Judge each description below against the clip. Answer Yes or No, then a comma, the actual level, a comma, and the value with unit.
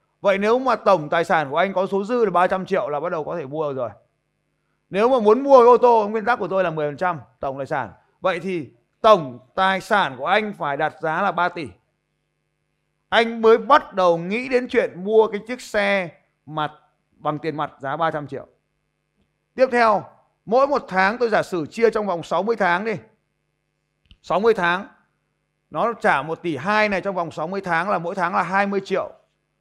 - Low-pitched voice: No, high, 190 Hz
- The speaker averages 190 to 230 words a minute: Yes, average, 205 wpm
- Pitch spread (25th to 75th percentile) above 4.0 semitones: Yes, average, 5.2 semitones